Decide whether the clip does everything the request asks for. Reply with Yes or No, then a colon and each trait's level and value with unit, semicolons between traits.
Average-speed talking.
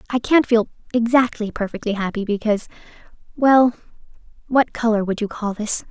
No: slow, 130 wpm